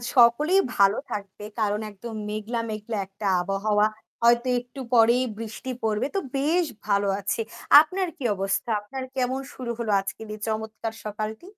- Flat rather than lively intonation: No, average, 3.0 semitones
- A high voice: Yes, high, 220 Hz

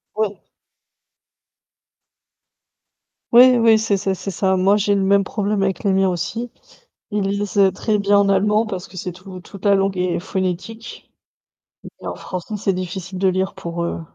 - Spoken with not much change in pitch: Yes, narrow, 1.9 semitones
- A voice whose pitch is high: Yes, high, 195 Hz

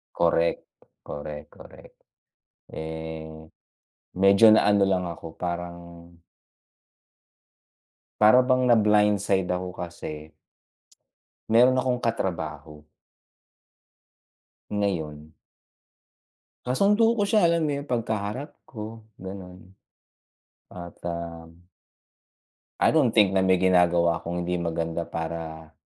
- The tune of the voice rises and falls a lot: No, average, 4.5 semitones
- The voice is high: No, very low, 90 Hz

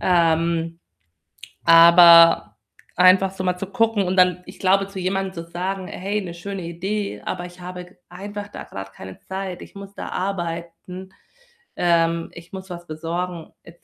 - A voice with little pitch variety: Yes, narrow, 2.2 semitones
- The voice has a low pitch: No, medium, 180 Hz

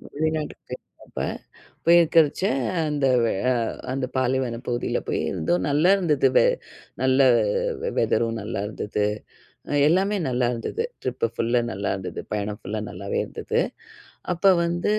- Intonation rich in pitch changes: Yes, wide, 6.7 semitones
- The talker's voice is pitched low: Yes, low, 130 Hz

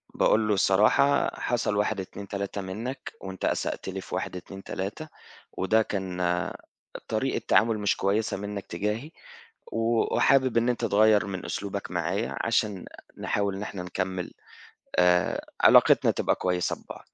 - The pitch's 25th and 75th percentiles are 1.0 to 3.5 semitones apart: Yes, average, 2.8 semitones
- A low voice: Yes, low, 100 Hz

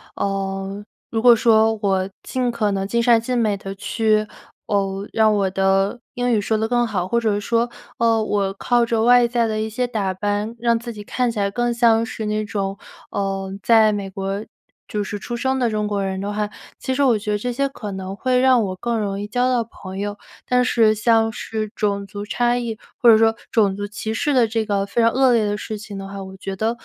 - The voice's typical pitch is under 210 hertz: No, high, 215 Hz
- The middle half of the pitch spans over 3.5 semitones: No, average, 2.8 semitones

